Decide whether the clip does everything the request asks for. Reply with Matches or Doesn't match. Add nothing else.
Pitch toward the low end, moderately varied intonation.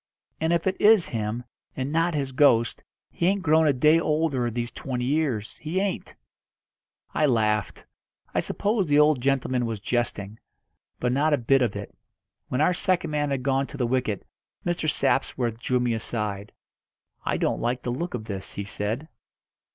Matches